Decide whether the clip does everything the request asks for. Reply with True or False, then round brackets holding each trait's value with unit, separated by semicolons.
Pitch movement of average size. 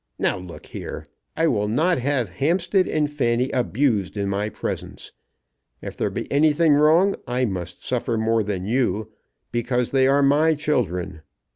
False (6.0 semitones)